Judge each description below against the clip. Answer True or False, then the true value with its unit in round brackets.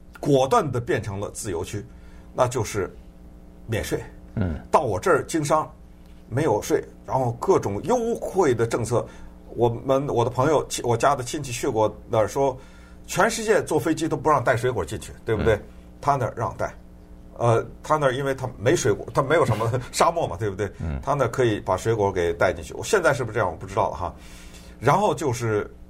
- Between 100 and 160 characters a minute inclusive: False (285 characters per minute)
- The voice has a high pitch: False (100 Hz)